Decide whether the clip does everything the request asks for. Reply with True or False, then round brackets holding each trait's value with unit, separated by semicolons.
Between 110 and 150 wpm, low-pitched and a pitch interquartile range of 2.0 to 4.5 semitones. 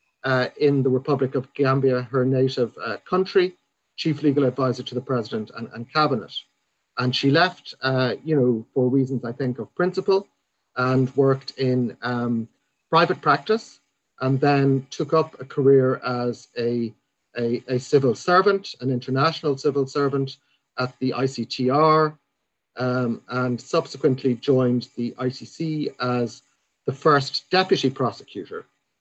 True (140 wpm; 130 Hz; 2.7 semitones)